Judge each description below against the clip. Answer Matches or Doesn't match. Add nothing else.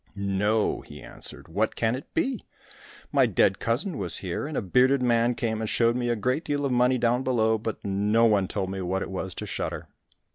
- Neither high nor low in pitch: Doesn't match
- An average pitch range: Matches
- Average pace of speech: Doesn't match